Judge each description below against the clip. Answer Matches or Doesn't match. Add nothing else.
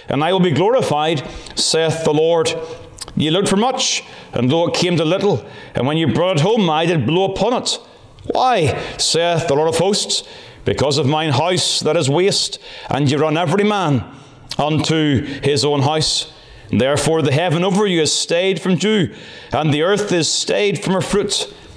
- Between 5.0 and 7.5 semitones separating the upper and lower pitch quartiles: Doesn't match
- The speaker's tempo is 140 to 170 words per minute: Doesn't match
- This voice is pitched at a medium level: Matches